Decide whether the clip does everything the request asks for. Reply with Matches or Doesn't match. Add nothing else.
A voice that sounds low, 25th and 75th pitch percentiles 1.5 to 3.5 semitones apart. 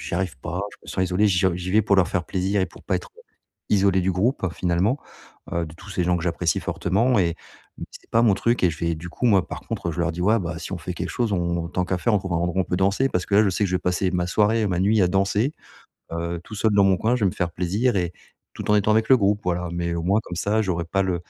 Matches